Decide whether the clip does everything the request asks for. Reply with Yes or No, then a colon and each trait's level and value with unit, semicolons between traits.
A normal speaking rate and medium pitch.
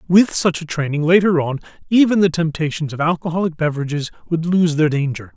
Yes: average, 180 wpm; medium, 165 Hz